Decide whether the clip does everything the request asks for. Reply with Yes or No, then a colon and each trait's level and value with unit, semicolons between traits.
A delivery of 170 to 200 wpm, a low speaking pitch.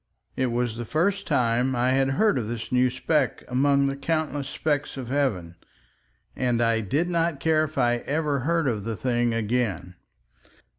Yes: average, 175 wpm; low, 130 Hz